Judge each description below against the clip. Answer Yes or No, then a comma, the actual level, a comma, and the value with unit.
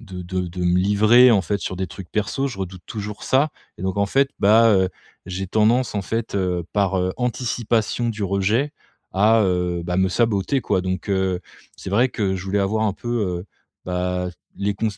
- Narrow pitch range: No, average, 3.3 semitones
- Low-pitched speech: Yes, low, 100 Hz